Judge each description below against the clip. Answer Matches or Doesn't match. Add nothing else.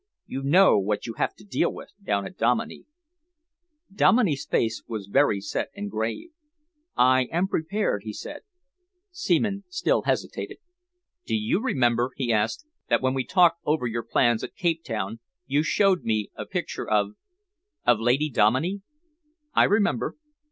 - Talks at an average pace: Matches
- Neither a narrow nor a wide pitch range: Doesn't match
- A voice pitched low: Matches